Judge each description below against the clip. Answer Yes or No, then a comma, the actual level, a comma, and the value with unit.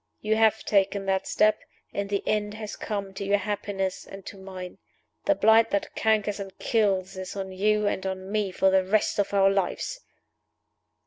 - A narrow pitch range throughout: Yes, narrow, 1.7 semitones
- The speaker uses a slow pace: No, average, 185 wpm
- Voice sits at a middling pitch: No, high, 200 Hz